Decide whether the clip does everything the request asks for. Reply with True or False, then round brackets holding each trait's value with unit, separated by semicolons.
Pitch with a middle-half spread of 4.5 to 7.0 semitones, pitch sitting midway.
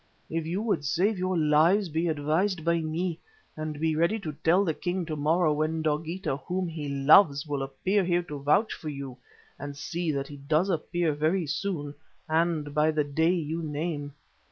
False (2.9 semitones; 160 Hz)